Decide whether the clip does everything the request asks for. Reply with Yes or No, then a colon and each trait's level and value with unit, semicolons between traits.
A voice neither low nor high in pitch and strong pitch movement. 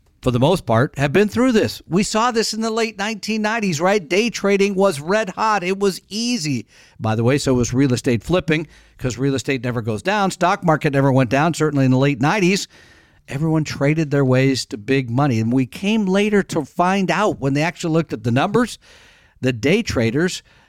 Yes: medium, 155 Hz; wide, 7.0 semitones